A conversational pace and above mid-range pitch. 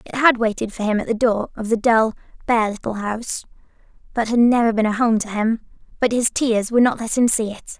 No: fast, 230 wpm; high, 225 Hz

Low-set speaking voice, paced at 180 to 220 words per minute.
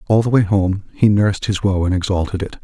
No: low, 100 Hz; fast, 250 wpm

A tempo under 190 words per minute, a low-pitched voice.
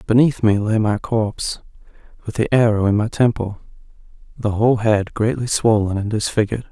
Yes: average, 160 wpm; low, 110 Hz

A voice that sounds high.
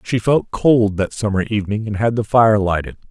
No: low, 110 Hz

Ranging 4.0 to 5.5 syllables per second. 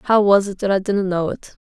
Yes: 4.6 syllables/s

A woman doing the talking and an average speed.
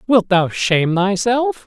No: male; average, 145 wpm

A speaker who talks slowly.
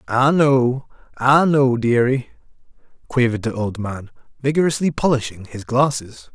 Yes: slow, 115 wpm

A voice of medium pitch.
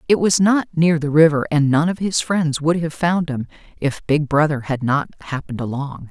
Yes: medium, 155 Hz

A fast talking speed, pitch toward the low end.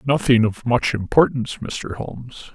No: average, 140 wpm; low, 120 Hz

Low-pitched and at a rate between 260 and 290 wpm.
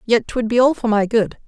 No: high, 225 Hz; fast, 285 wpm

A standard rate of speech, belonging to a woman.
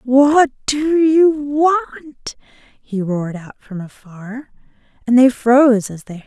Yes: average, 145 wpm; female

